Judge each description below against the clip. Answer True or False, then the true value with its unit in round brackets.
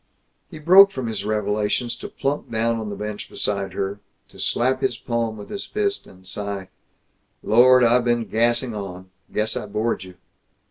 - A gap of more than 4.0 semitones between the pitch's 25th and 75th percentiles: False (3.2 semitones)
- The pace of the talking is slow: False (175 wpm)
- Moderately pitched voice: False (110 Hz)